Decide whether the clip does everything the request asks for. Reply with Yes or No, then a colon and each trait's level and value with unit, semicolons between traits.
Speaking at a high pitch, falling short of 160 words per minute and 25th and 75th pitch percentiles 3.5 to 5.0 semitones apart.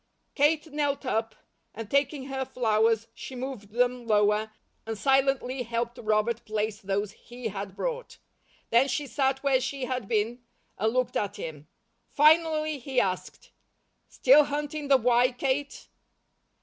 Yes: very high, 250 Hz; average, 140 wpm; average, 4.0 semitones